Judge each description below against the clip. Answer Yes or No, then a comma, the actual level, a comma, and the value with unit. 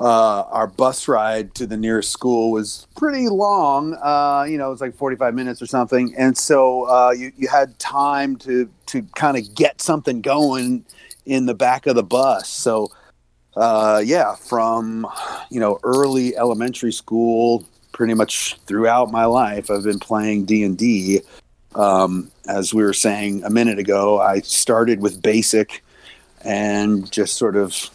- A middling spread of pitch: Yes, average, 3.4 semitones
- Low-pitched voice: Yes, low, 115 Hz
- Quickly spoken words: No, average, 165 wpm